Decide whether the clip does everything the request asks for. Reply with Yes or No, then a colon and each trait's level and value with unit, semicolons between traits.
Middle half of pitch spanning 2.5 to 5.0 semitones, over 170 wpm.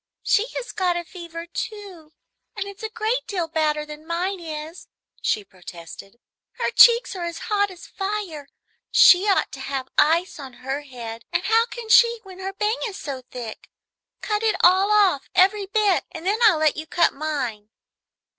No: wide, 5.4 semitones; average, 185 wpm